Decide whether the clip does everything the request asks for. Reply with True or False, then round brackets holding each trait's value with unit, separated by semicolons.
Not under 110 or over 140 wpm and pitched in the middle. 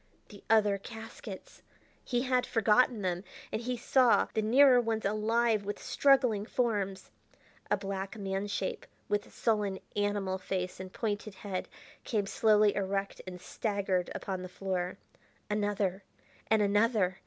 False (135 wpm; 205 Hz)